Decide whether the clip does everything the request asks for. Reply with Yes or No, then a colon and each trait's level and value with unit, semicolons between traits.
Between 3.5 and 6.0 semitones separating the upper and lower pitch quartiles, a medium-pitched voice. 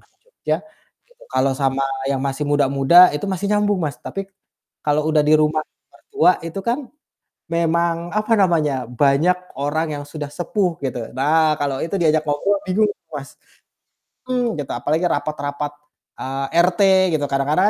Yes: average, 4.2 semitones; medium, 155 Hz